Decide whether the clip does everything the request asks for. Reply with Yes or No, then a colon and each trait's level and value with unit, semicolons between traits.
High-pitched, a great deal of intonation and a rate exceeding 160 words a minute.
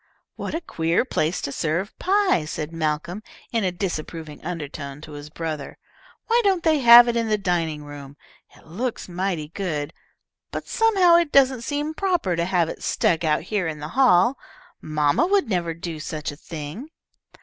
No: medium, 175 Hz; wide, 8.3 semitones; average, 175 wpm